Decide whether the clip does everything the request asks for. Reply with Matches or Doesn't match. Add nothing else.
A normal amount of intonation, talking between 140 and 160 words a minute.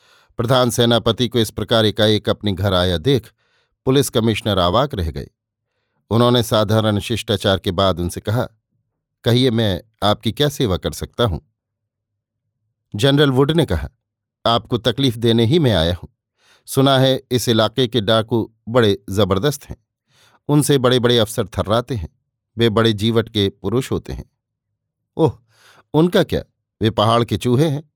Matches